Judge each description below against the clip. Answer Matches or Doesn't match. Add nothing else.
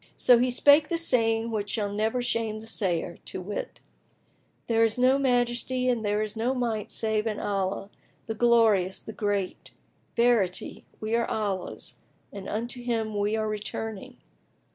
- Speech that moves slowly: Doesn't match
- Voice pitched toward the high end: Matches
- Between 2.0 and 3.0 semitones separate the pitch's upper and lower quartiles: Matches